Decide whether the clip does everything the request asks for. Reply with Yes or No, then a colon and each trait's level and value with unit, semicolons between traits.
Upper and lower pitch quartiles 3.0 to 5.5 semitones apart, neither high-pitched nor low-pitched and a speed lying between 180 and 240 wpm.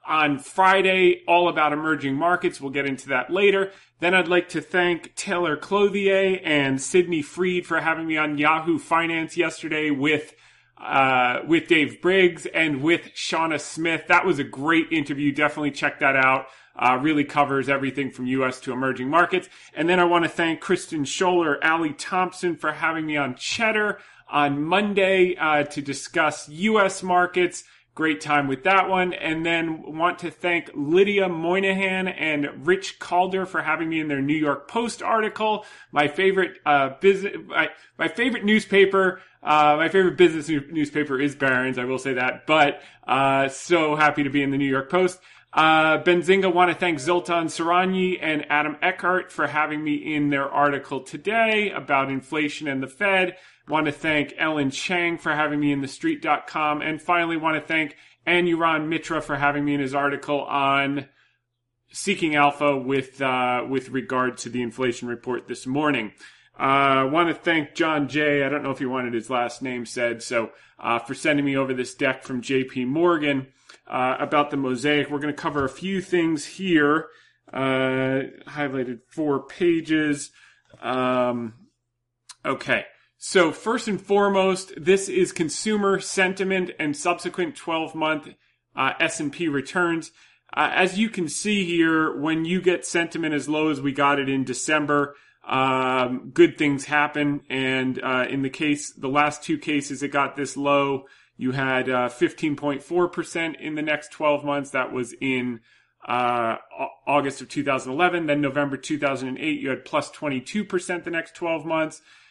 No: average, 4.2 semitones; medium, 155 Hz; average, 170 wpm